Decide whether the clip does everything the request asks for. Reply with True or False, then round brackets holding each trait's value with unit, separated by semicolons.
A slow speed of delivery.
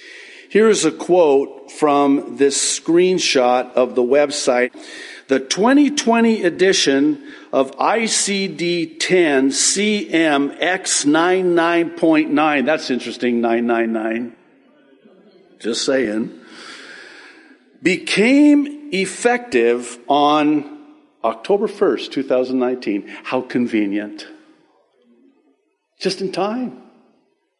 True (70 wpm)